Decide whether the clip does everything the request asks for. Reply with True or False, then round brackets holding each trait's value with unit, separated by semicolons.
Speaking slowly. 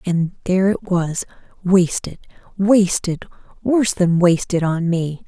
True (115 wpm)